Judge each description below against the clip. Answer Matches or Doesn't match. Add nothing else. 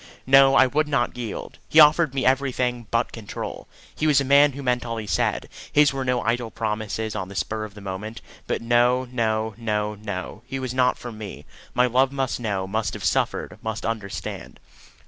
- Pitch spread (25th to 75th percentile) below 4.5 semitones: Matches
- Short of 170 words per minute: Doesn't match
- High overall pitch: Doesn't match